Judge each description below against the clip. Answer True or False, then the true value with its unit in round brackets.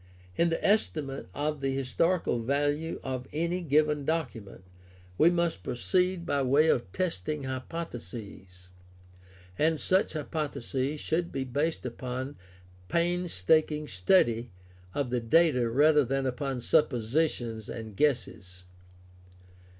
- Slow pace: True (110 wpm)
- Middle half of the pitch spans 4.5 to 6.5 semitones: True (4.9 semitones)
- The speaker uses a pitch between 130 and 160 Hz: True (140 Hz)